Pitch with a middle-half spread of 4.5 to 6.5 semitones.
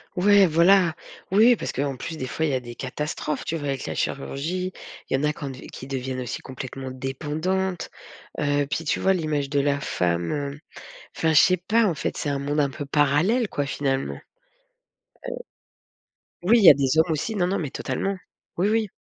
Yes: average, 4.8 semitones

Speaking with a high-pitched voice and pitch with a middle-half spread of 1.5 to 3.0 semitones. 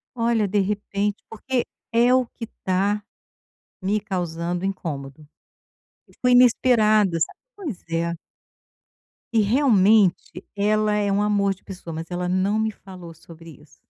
No: high, 200 Hz; average, 3.4 semitones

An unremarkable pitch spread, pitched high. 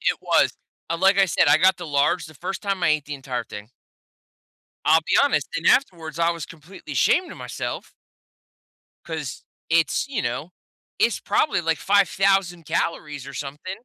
No: average, 4.3 semitones; medium, 165 Hz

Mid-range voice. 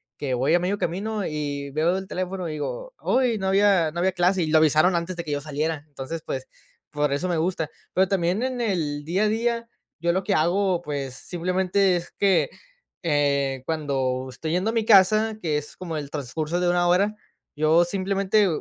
Yes: medium, 175 Hz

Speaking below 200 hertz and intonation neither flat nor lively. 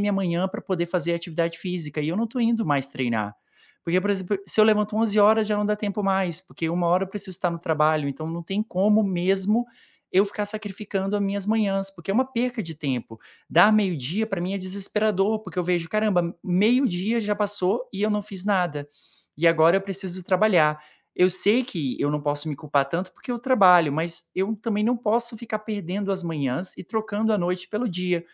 Yes: high, 190 Hz; average, 3.8 semitones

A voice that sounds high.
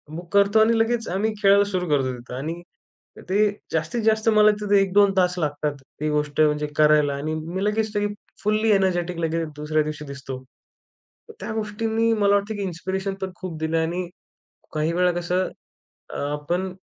No: medium, 180 Hz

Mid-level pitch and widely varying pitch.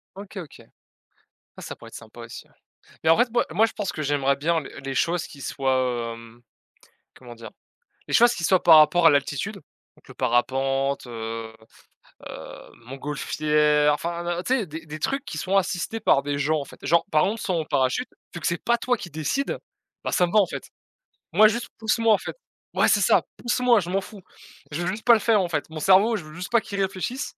Yes: medium, 170 Hz; wide, 6.4 semitones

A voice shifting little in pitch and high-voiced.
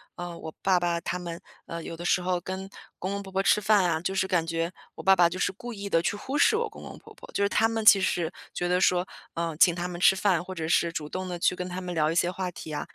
No: narrow, 2.1 semitones; medium, 180 Hz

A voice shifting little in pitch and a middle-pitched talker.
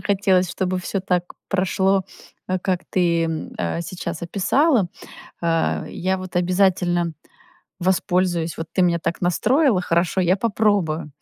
Yes: narrow, 2.0 semitones; medium, 180 Hz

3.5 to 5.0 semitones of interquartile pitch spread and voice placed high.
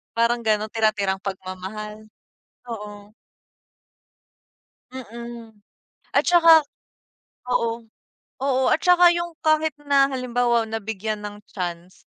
Yes: average, 4.0 semitones; high, 230 Hz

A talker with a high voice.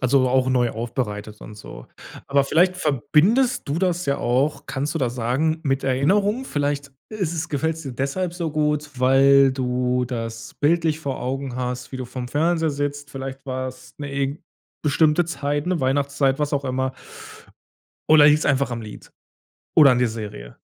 No: medium, 140 Hz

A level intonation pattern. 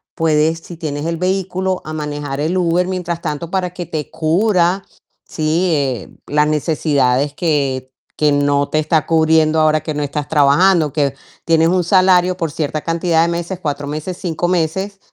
No: average, 3.0 semitones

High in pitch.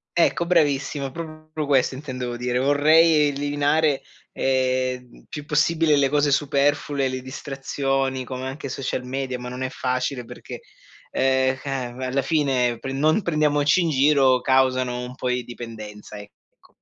No: low, 135 Hz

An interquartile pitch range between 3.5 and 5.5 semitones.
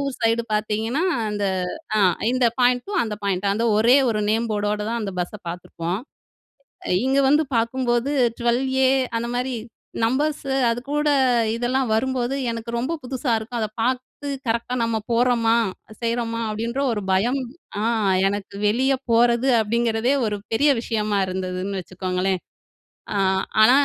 No: average, 3.0 semitones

